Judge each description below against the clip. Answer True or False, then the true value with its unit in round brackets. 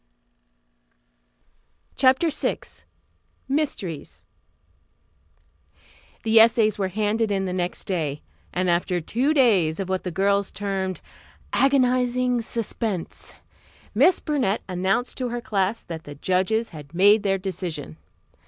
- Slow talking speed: True (115 wpm)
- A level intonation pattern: False (4.6 semitones)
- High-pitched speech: True (200 Hz)